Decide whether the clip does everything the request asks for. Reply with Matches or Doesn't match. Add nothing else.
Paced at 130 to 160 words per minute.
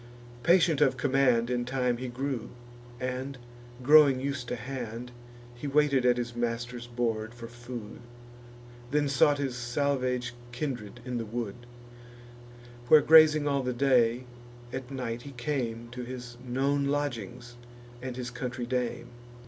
Matches